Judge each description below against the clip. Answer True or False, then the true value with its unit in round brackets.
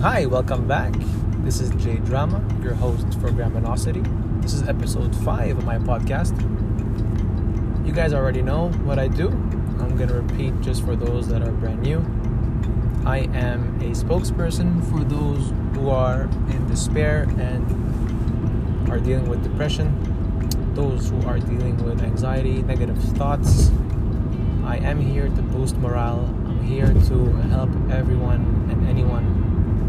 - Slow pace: False (145 wpm)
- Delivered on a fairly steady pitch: True (1.9 semitones)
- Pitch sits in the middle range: False (110 Hz)